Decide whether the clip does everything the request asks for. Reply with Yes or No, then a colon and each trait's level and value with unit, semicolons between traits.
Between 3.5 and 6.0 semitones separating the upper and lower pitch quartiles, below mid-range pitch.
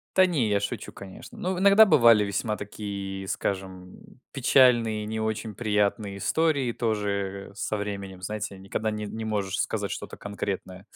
No: average, 2.7 semitones; low, 105 Hz